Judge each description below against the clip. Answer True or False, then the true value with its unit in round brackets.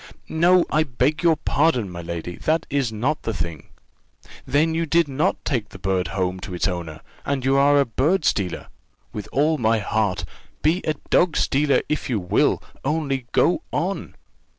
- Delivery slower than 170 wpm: False (175 wpm)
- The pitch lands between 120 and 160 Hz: True (135 Hz)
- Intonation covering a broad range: True (8.0 semitones)